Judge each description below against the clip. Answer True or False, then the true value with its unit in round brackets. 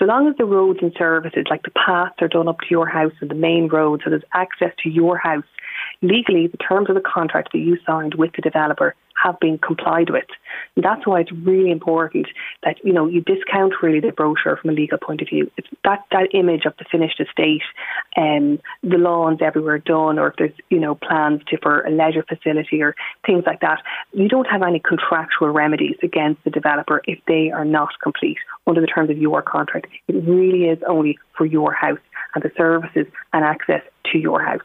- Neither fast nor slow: False (215 wpm)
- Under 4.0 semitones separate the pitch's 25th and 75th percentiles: True (2.5 semitones)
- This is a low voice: False (165 Hz)